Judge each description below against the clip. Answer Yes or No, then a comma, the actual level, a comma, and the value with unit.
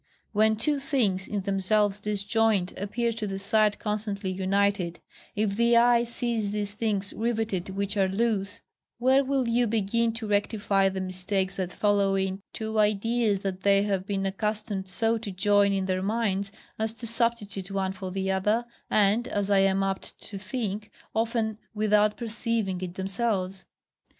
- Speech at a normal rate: Yes, average, 160 wpm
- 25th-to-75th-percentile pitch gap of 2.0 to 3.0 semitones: Yes, narrow, 2.5 semitones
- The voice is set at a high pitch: Yes, high, 205 Hz